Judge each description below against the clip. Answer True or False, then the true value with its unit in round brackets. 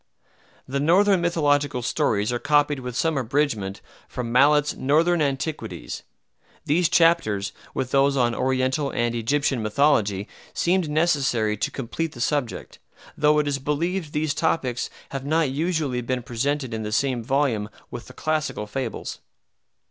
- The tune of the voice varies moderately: True (3.9 semitones)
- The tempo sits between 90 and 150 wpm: True (140 wpm)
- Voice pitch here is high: False (140 Hz)